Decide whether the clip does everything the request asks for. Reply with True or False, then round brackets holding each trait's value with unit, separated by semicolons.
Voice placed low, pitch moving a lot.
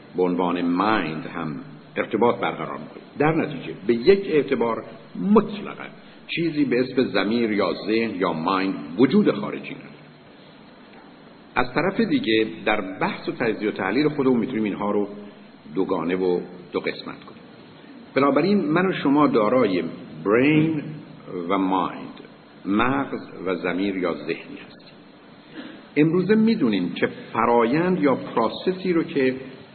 True (130 Hz; 7.9 semitones)